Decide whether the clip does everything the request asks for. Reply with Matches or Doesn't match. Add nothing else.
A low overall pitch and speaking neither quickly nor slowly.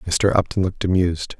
Matches